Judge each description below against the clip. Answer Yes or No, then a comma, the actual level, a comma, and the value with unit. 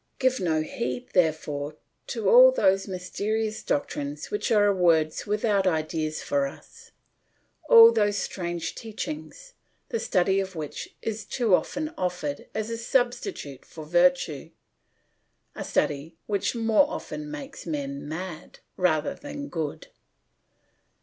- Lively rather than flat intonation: Yes, wide, 7.5 semitones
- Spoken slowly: Yes, slow, 125 wpm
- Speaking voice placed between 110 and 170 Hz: No, high, 190 Hz